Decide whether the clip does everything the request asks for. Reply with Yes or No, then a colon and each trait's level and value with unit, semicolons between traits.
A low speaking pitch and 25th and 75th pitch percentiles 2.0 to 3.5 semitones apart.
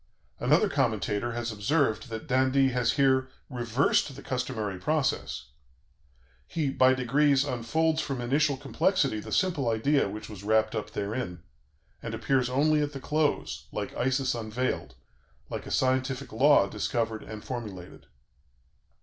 No: low, 130 Hz; average, 4.0 semitones